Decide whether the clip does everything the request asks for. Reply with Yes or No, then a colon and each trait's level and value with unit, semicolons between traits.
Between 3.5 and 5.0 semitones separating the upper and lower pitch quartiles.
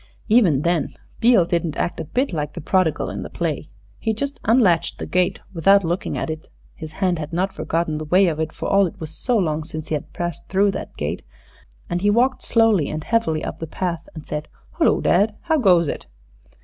Yes: average, 4.2 semitones